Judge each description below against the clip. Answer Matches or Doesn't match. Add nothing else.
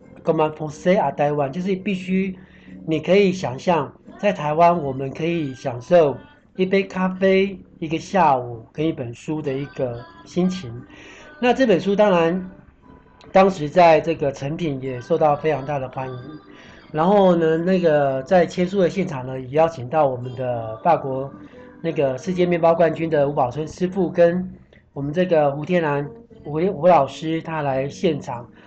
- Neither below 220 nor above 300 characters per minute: Matches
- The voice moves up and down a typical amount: Matches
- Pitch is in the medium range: Matches